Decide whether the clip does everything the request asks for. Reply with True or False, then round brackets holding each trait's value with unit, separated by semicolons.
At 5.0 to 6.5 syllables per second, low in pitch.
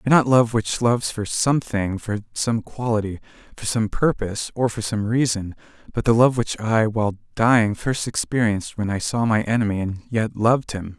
True (5.3 syllables/s; 110 Hz)